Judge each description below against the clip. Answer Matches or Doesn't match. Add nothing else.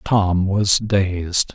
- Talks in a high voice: Doesn't match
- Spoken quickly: Doesn't match